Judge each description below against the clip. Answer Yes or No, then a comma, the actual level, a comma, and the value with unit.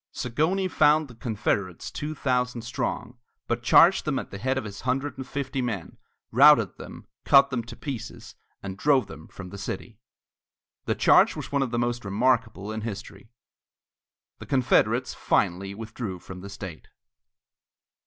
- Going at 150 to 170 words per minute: Yes, average, 160 wpm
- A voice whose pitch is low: Yes, low, 120 Hz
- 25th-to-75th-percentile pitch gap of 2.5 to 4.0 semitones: No, average, 5.1 semitones